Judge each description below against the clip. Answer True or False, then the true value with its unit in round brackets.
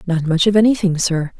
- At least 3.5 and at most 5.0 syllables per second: False (5.7 syllables/s)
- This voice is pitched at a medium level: True (180 Hz)